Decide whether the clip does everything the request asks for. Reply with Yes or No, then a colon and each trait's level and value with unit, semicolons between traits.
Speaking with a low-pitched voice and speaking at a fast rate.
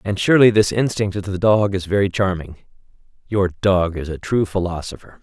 No: very low, 95 Hz; average, 170 wpm